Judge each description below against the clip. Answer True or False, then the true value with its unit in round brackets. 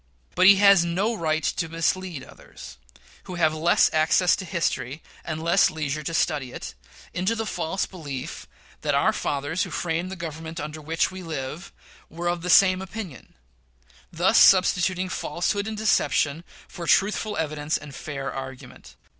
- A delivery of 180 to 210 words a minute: False (160 wpm)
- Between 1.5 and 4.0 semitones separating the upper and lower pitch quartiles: True (3.3 semitones)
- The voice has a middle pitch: True (170 Hz)